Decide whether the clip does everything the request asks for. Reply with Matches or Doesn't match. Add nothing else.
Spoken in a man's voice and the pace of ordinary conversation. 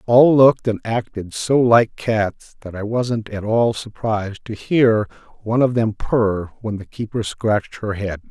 Matches